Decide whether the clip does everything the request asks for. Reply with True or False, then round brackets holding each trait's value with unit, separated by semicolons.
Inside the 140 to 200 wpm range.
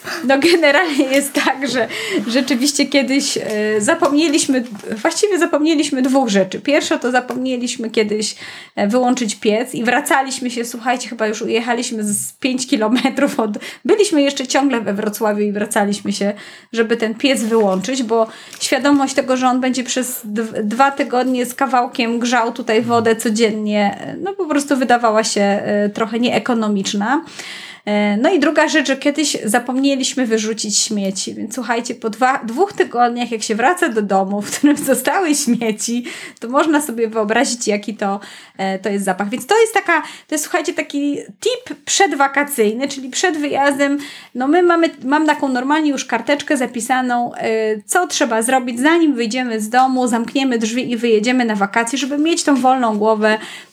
True (155 wpm)